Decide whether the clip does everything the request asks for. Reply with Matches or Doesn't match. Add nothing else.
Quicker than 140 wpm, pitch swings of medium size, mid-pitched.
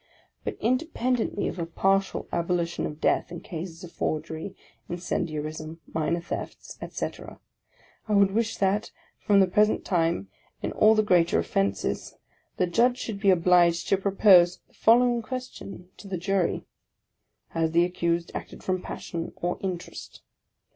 Matches